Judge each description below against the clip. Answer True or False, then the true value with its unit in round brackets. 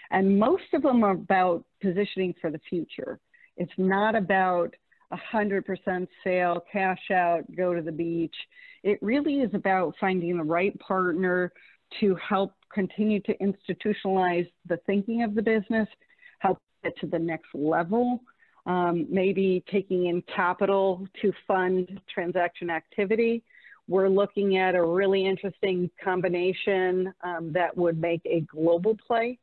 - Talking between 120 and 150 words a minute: True (140 wpm)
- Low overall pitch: False (190 Hz)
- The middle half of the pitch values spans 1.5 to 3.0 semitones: True (2.6 semitones)